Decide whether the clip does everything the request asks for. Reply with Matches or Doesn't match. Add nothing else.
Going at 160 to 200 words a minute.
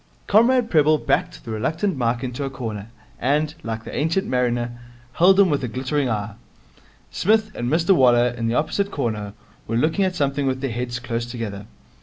Matches